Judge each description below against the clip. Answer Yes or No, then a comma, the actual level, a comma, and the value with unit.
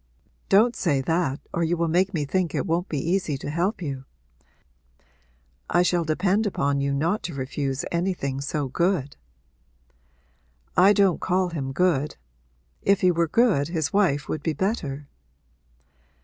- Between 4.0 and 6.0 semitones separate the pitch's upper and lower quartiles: Yes, average, 4.6 semitones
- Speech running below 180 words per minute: Yes, average, 150 wpm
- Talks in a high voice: No, medium, 170 Hz